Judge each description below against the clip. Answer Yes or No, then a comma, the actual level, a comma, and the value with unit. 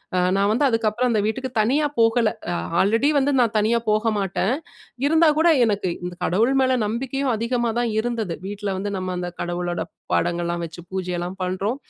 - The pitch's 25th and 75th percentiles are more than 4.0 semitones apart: Yes, average, 4.6 semitones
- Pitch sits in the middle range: No, high, 215 Hz